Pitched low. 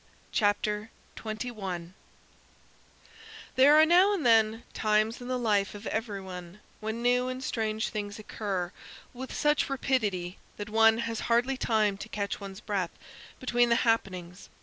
No: high, 220 Hz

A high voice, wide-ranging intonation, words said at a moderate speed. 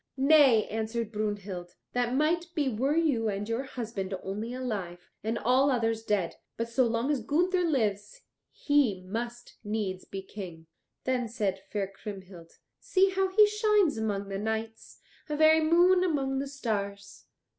Yes: high, 230 Hz; wide, 5.8 semitones; average, 155 wpm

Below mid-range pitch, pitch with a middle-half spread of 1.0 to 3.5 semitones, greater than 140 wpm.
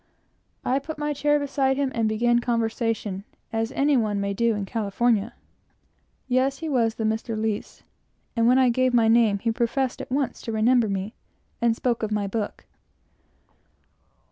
No: high, 235 Hz; average, 2.9 semitones; average, 170 wpm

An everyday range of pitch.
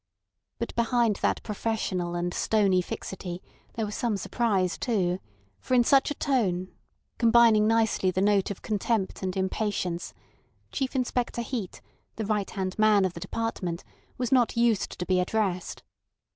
Yes: average, 3.9 semitones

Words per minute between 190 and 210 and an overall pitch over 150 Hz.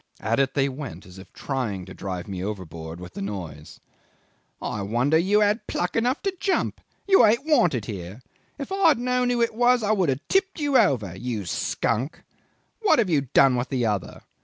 No: average, 200 wpm; low, 135 Hz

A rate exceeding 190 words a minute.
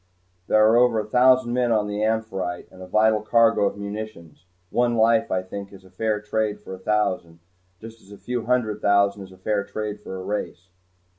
Yes: average, 200 wpm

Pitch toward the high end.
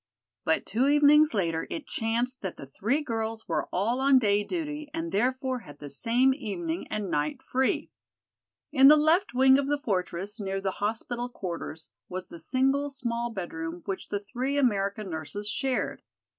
Yes: high, 230 Hz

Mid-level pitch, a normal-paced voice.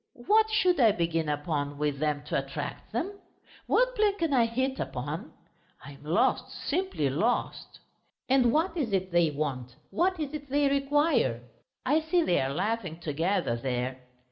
No: high, 210 Hz; average, 165 wpm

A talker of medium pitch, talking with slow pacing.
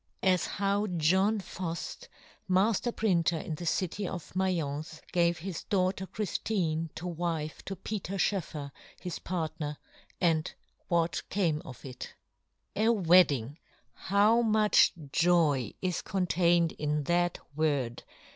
Yes: medium, 175 Hz; slow, 120 wpm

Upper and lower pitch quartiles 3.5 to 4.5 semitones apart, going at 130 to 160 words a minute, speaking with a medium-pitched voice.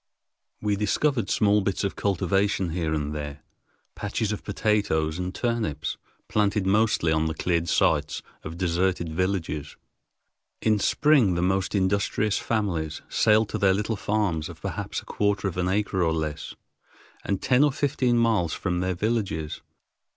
No: average, 4.1 semitones; average, 150 wpm; very low, 95 Hz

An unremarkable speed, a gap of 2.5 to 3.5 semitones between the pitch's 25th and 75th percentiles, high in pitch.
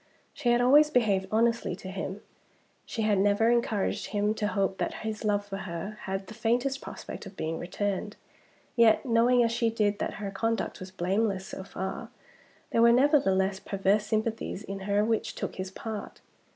Yes: average, 180 wpm; average, 2.9 semitones; high, 210 Hz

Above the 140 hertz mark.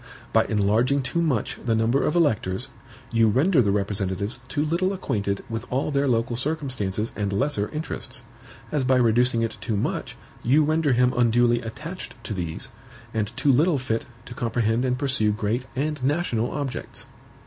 No: low, 120 Hz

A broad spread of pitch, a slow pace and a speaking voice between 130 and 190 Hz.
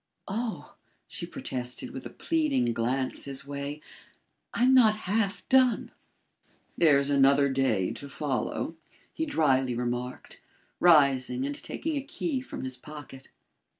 Yes: wide, 8.7 semitones; slow, 125 wpm; medium, 140 Hz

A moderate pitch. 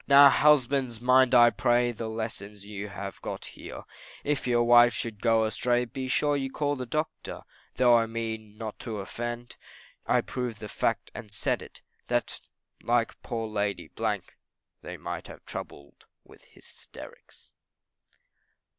No: low, 120 Hz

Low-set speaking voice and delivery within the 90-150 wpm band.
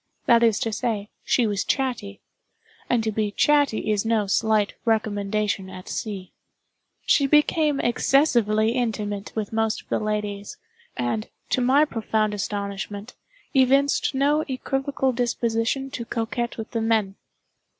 No: high, 225 Hz; slow, 135 wpm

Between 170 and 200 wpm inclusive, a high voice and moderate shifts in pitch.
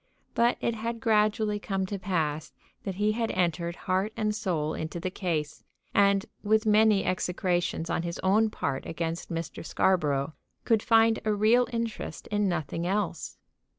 No: average, 155 wpm; high, 195 Hz; average, 4.1 semitones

